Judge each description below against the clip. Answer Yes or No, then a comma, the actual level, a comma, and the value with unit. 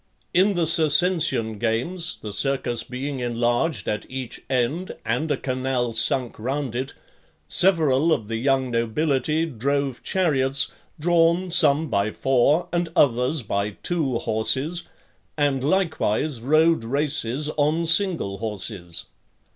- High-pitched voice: No, low, 135 Hz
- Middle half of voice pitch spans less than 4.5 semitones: No, average, 5.3 semitones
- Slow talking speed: Yes, slow, 125 wpm